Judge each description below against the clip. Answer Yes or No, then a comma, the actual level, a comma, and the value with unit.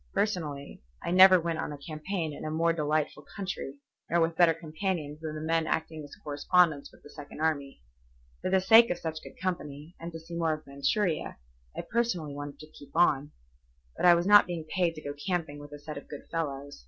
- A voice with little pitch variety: No, average, 3.0 semitones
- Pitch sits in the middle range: Yes, medium, 160 Hz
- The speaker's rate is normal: No, fast, 215 wpm